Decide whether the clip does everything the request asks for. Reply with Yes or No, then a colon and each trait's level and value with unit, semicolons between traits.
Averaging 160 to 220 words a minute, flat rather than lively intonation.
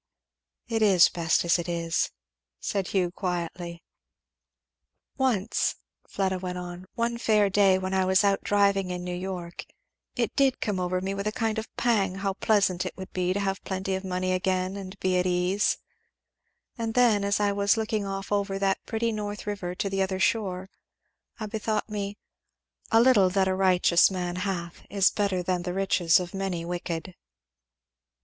Yes: average, 175 wpm; narrow, 2.1 semitones